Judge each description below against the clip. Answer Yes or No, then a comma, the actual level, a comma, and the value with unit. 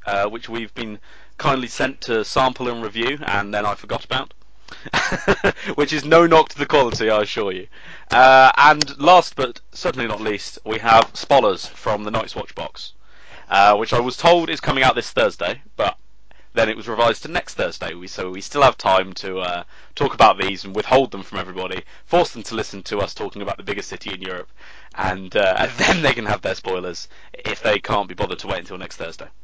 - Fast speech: Yes, fast, 215 wpm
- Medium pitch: No, low, 110 Hz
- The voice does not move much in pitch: No, average, 4.5 semitones